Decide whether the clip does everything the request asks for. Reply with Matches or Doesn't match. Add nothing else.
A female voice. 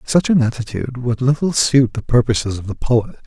Doesn't match